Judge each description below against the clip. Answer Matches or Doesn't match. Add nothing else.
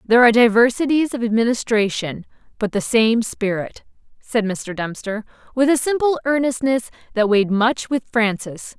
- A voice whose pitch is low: Doesn't match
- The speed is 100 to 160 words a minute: Matches